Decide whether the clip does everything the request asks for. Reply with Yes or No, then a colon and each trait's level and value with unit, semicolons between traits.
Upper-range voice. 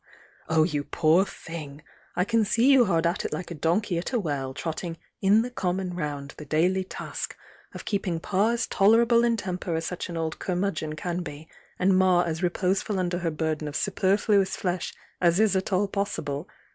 No: medium, 180 Hz